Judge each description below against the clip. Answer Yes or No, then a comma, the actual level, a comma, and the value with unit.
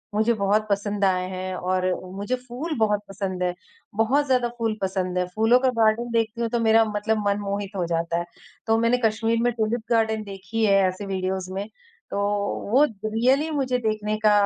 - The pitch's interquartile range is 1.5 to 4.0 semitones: Yes, average, 2.8 semitones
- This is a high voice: Yes, high, 215 Hz